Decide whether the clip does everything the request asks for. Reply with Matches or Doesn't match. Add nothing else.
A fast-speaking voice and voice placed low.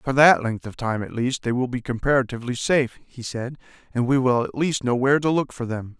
Matches